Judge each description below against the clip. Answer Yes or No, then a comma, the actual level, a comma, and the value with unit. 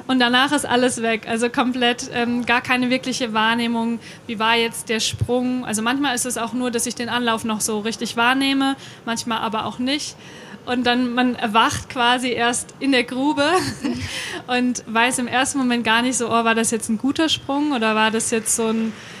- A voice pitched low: No, high, 240 Hz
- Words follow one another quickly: Yes, fast, 205 wpm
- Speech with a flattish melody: Yes, narrow, 1.7 semitones